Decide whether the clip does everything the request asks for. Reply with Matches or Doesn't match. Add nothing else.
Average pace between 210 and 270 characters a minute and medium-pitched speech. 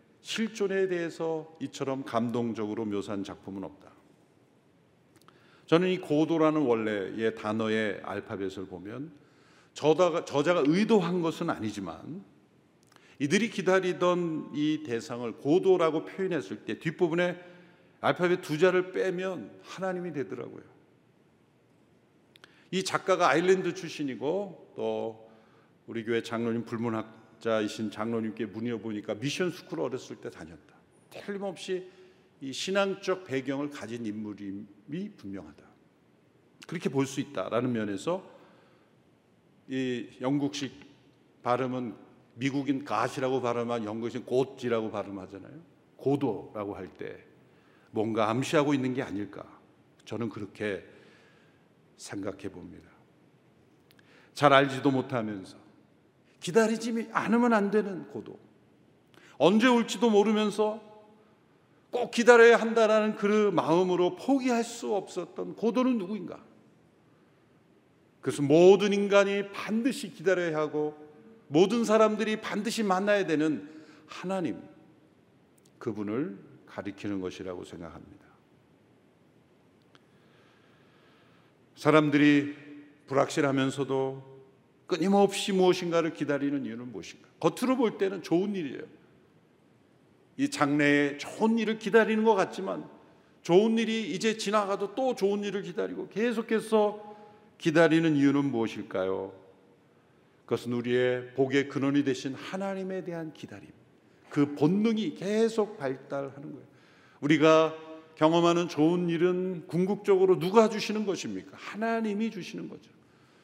Matches